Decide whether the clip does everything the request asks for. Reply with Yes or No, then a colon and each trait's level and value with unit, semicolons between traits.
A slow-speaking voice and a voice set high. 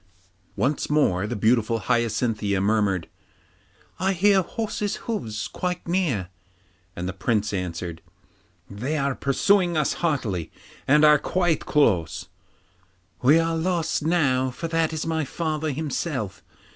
No: slow, 125 wpm; medium, 140 Hz